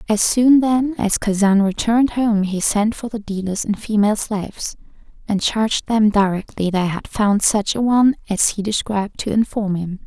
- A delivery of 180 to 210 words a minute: Yes, average, 185 wpm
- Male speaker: No, female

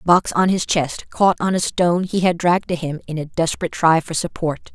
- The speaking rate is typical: No, fast, 255 wpm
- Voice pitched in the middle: Yes, medium, 170 Hz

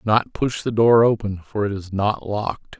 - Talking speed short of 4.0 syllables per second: No, 4.9 syllables/s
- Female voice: No, male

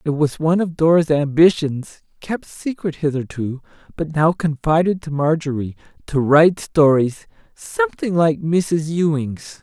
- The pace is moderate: No, slow, 130 wpm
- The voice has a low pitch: No, medium, 155 Hz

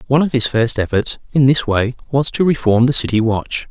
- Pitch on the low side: Yes, low, 125 Hz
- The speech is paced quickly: Yes, fast, 225 wpm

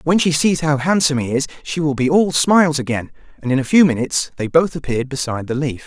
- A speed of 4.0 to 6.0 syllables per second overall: No, 6.5 syllables/s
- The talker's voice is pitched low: No, medium, 145 Hz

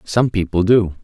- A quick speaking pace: No, average, 175 wpm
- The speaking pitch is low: Yes, low, 100 Hz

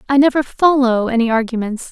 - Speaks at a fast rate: No, average, 155 wpm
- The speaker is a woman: Yes, female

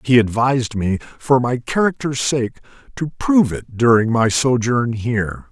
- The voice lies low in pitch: Yes, low, 125 Hz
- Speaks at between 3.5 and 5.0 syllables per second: Yes, 4.6 syllables/s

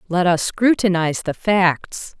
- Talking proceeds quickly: No, slow, 135 wpm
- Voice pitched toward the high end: No, medium, 180 Hz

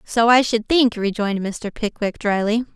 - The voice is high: Yes, high, 220 Hz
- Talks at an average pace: Yes, average, 175 wpm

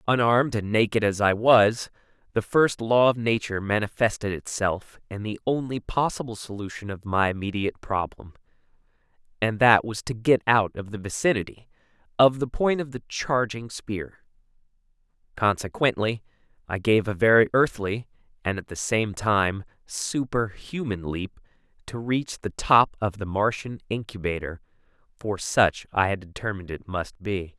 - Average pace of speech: Yes, average, 145 wpm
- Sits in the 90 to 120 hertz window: Yes, low, 110 Hz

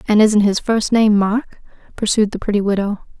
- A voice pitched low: No, high, 210 Hz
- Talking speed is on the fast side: No, average, 190 wpm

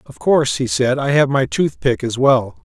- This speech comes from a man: Yes, male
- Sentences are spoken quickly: Yes, fast, 220 wpm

